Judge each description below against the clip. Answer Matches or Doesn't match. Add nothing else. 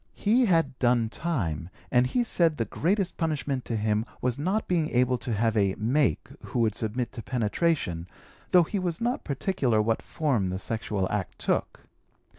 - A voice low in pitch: Matches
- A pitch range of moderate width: Doesn't match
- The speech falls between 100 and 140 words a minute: Doesn't match